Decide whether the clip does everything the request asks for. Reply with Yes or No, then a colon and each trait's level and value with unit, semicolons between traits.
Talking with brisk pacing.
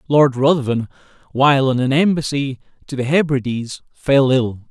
No: average, 140 wpm